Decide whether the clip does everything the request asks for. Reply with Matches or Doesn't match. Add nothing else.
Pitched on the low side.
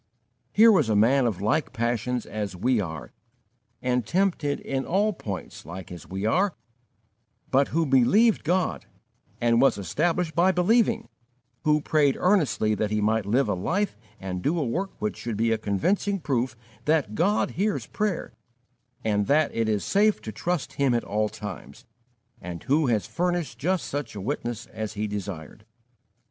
Matches